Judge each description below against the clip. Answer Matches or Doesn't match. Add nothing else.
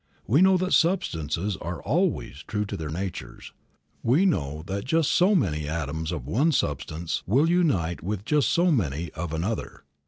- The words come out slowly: Doesn't match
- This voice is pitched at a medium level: Doesn't match